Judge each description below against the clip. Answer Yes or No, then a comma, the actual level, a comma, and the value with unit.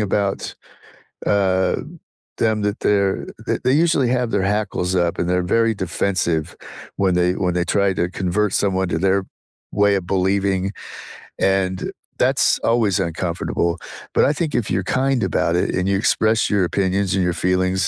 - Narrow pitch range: Yes, narrow, 2.2 semitones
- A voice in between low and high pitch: No, very low, 95 Hz